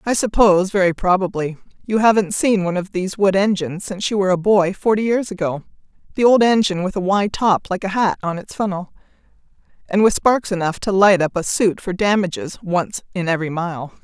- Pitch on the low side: No, high, 190 Hz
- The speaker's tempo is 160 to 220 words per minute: Yes, average, 200 wpm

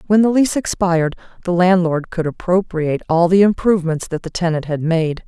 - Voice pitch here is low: No, medium, 175 Hz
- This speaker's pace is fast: No, average, 180 wpm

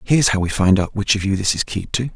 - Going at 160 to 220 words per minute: No, fast, 335 wpm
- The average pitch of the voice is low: Yes, low, 100 Hz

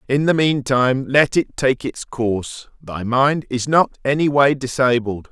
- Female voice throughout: No, male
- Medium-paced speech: Yes, average, 180 wpm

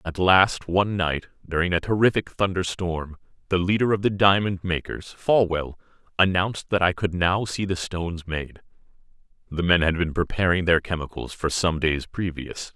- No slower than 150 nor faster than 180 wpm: Yes, average, 160 wpm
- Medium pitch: No, very low, 90 Hz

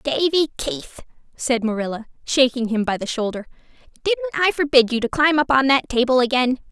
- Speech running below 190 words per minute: Yes, average, 180 wpm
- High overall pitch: Yes, very high, 265 Hz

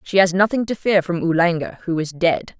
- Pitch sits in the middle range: Yes, medium, 175 Hz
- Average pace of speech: No, fast, 230 wpm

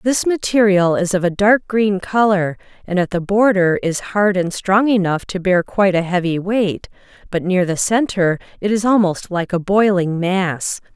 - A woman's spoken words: Yes, female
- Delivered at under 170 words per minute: No, average, 185 wpm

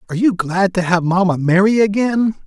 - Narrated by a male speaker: Yes, male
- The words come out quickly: No, average, 195 wpm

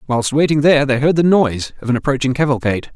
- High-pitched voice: No, low, 135 Hz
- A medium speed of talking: No, fast, 225 wpm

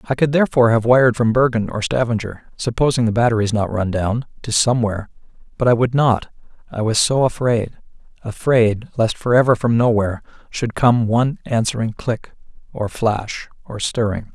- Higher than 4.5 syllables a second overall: Yes, 5.4 syllables/s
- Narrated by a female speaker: No, male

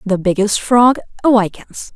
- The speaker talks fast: No, slow, 125 wpm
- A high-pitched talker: Yes, high, 210 Hz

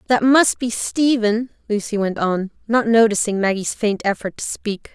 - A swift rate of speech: No, average, 170 wpm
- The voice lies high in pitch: Yes, high, 220 Hz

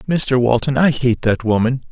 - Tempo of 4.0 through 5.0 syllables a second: Yes, 4.7 syllables/s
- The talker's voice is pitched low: Yes, low, 130 Hz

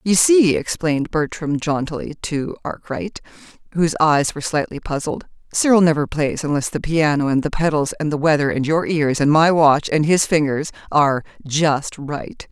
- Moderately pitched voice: Yes, medium, 155 Hz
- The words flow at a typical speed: Yes, average, 175 wpm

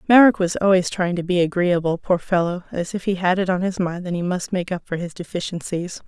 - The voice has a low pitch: No, medium, 180 Hz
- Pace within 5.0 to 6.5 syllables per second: Yes, 5.7 syllables/s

